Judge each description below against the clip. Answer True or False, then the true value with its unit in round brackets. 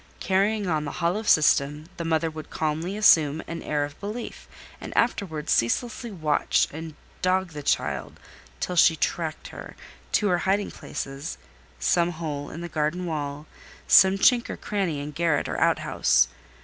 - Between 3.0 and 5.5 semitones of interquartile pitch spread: True (3.9 semitones)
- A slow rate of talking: False (155 wpm)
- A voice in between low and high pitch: True (165 Hz)